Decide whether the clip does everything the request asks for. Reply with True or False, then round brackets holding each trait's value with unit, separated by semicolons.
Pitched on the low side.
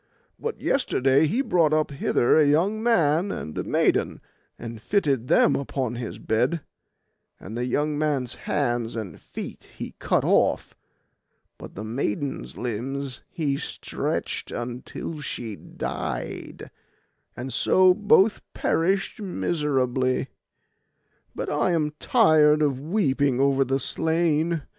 False (145 Hz)